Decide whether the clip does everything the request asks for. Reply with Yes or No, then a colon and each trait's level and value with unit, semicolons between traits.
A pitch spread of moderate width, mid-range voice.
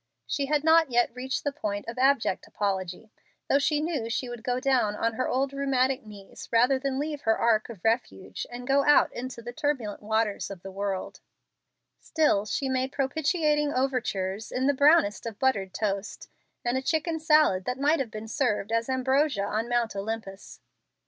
No: average, 4.4 semitones; very high, 250 Hz